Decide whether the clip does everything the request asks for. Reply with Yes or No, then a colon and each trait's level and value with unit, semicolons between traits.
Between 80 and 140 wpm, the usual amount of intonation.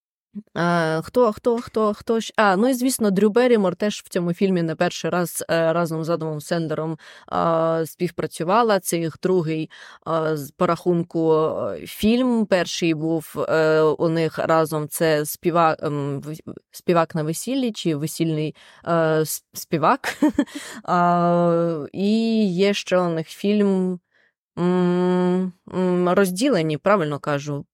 Yes: average, 115 wpm; average, 3.9 semitones